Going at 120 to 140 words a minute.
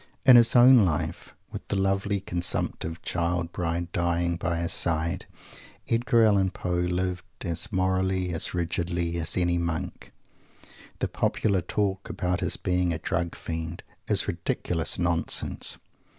Yes: slow, 135 wpm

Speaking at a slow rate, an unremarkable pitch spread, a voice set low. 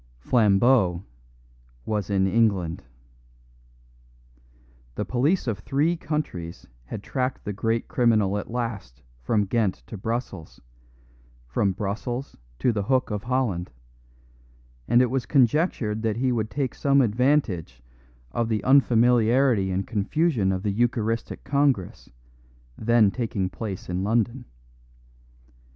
Yes: slow, 120 wpm; average, 4.3 semitones; low, 115 Hz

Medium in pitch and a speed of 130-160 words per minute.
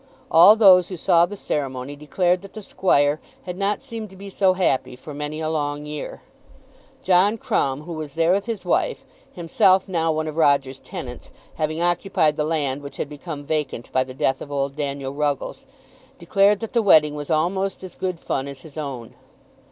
No: medium, 155 Hz; average, 190 wpm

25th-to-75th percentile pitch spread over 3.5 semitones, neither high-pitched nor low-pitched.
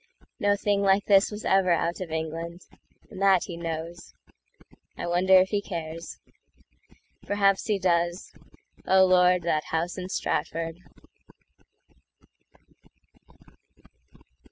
No: narrow, 2.5 semitones; medium, 180 Hz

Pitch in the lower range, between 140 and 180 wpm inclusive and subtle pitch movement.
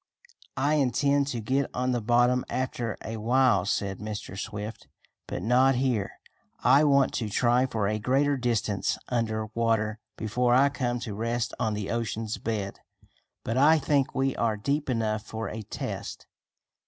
No: low, 120 Hz; average, 160 wpm; average, 3.3 semitones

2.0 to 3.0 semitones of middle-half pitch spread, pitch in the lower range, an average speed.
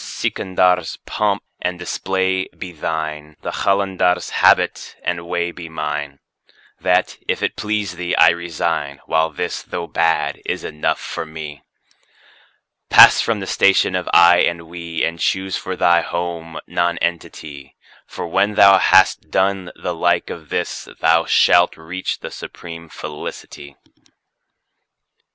No: narrow, 2.4 semitones; very low, 85 Hz; slow, 130 wpm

